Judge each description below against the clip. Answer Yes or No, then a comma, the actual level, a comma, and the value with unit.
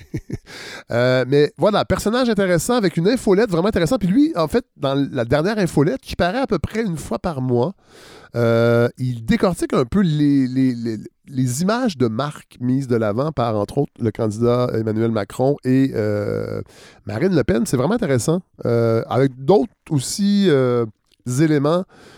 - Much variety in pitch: Yes, wide, 7.6 semitones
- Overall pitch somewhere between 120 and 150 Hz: Yes, medium, 140 Hz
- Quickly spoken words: No, average, 170 wpm